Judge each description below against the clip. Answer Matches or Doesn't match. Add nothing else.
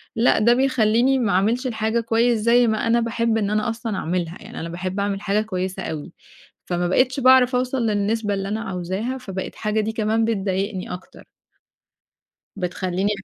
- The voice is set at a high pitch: Matches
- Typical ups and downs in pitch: Matches